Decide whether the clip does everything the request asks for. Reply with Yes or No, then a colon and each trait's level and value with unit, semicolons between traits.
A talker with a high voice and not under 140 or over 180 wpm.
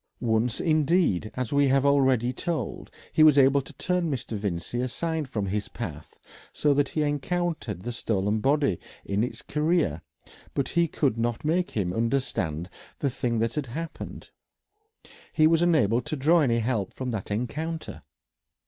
No: low, 135 Hz; average, 160 wpm